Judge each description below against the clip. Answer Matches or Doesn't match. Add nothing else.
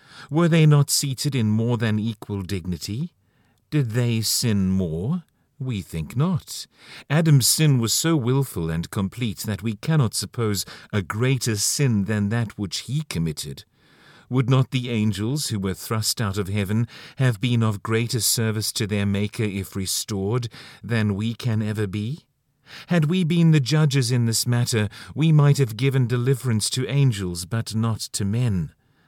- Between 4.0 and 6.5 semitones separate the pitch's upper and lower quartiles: Matches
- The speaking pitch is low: Matches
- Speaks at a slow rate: Doesn't match